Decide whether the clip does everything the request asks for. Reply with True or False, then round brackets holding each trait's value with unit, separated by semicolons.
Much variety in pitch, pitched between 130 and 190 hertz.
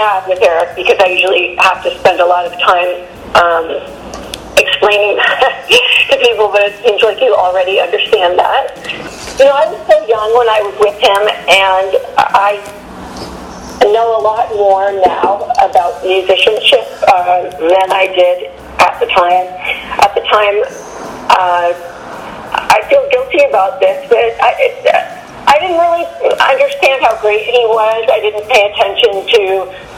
False (7.8 semitones; 210 Hz)